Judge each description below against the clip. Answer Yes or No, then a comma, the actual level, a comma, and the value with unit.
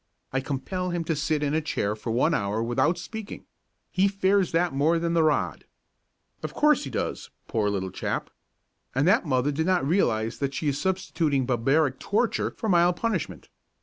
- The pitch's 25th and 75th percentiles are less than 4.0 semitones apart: No, wide, 5.4 semitones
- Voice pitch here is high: No, medium, 155 Hz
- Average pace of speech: Yes, average, 185 wpm